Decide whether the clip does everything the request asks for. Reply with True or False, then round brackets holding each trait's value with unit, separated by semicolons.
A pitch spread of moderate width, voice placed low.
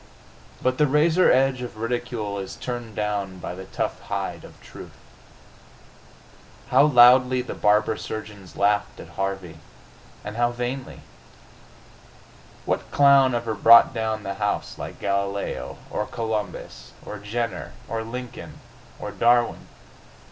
True (3.4 semitones; 110 Hz)